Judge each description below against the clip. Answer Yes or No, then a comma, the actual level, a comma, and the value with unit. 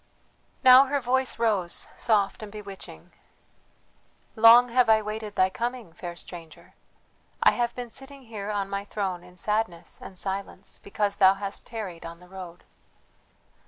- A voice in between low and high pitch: No, high, 205 Hz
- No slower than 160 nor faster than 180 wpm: No, average, 150 wpm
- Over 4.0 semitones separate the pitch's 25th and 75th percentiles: No, average, 3.7 semitones